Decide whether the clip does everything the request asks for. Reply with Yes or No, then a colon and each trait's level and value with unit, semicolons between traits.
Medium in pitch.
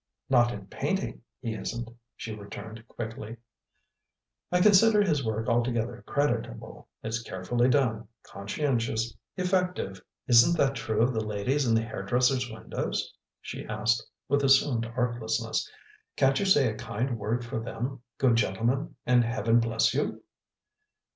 No: low, 120 Hz